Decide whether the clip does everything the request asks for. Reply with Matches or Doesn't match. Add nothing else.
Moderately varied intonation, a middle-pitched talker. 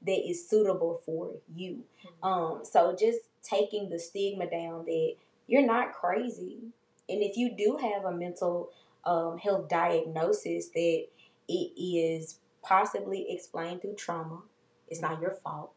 Matches